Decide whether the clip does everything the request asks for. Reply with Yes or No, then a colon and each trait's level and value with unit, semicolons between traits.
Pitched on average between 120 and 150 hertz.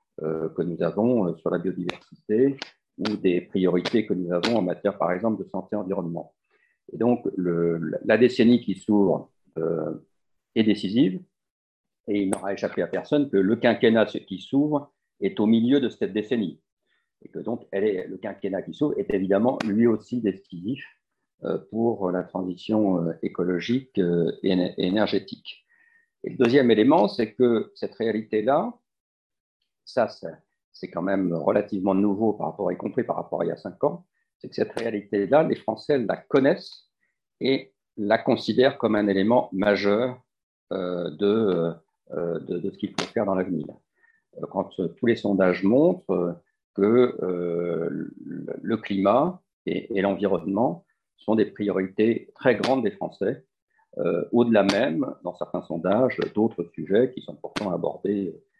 No: low, 100 Hz